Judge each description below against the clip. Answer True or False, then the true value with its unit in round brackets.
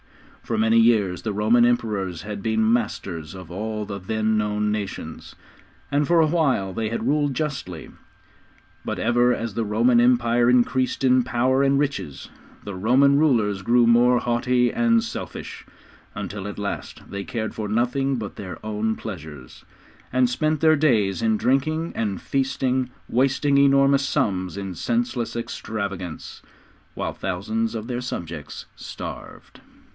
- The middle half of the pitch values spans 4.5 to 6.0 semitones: False (4.1 semitones)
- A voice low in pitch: True (115 Hz)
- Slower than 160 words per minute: True (145 wpm)